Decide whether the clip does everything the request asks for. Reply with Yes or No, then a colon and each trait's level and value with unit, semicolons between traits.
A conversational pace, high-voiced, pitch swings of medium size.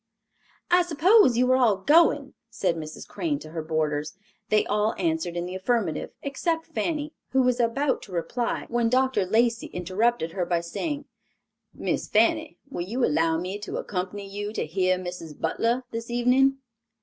No: average, 165 wpm; high, 220 Hz; wide, 6.6 semitones